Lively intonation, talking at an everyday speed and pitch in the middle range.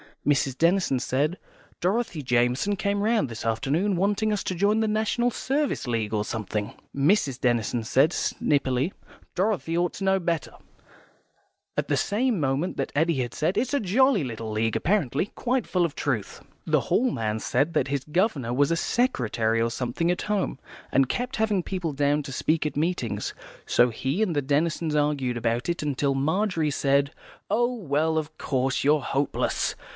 Yes: wide, 6.9 semitones; average, 170 wpm; medium, 150 Hz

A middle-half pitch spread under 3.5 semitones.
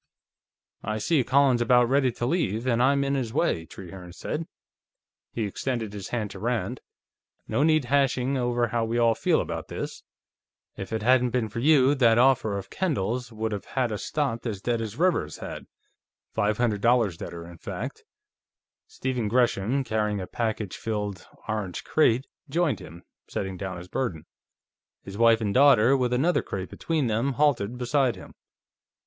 No: average, 4.0 semitones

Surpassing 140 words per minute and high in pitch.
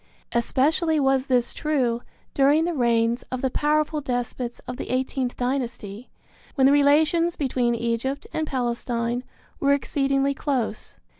No: slow, 135 wpm; very high, 265 Hz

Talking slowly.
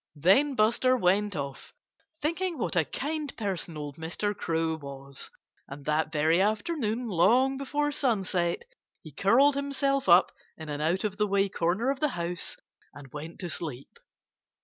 No: average, 155 wpm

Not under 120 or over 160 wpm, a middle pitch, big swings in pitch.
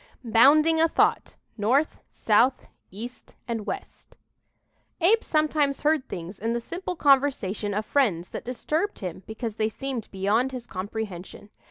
No: average, 140 wpm; high, 240 Hz; wide, 5.9 semitones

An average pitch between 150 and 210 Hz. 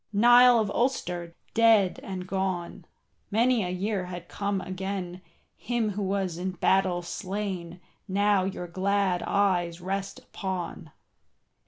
Yes: high, 190 Hz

